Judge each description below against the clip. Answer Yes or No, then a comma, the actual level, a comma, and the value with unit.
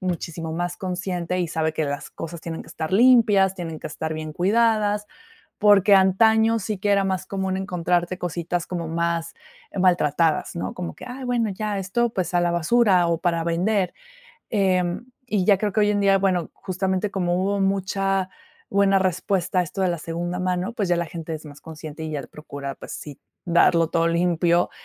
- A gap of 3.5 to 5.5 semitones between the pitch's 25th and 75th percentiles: No, average, 2.8 semitones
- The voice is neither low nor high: Yes, medium, 180 Hz